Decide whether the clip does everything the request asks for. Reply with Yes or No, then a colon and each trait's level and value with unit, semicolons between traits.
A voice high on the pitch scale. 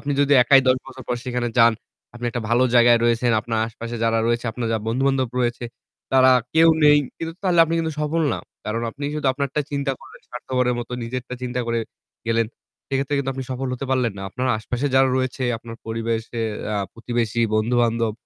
No: low, 125 Hz